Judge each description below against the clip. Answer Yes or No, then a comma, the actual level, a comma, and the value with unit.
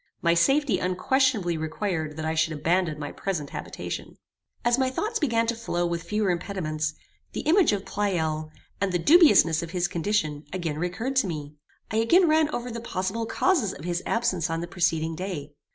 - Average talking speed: Yes, average, 185 wpm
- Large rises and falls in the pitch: Yes, wide, 6.2 semitones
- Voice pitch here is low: No, medium, 180 Hz